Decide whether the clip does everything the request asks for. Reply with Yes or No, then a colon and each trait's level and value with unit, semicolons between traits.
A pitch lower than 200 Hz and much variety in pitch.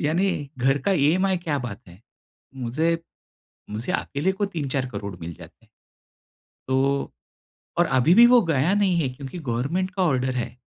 Yes: medium, 140 Hz; wide, 6.2 semitones